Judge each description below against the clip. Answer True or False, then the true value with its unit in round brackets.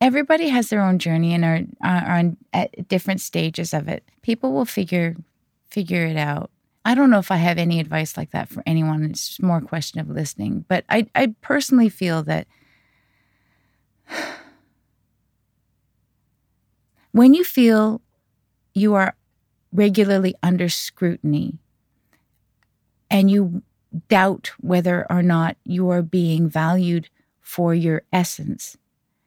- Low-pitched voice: False (175 Hz)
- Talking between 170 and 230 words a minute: False (135 wpm)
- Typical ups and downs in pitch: True (4.1 semitones)